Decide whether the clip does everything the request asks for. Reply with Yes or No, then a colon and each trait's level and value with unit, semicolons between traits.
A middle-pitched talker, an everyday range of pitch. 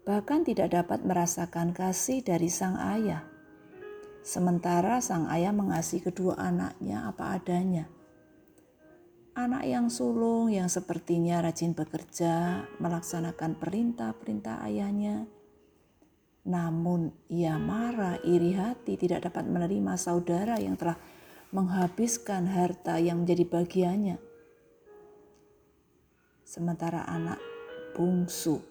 Yes: medium, 175 Hz; average, 4.2 semitones